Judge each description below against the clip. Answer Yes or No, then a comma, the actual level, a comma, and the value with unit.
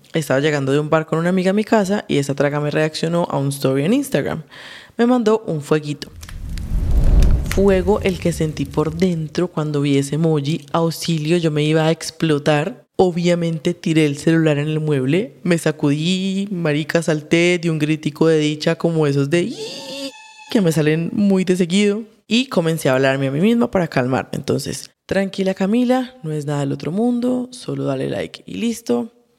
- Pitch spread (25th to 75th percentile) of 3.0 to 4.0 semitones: No, average, 4.6 semitones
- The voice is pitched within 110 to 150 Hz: No, medium, 165 Hz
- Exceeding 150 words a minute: Yes, average, 185 wpm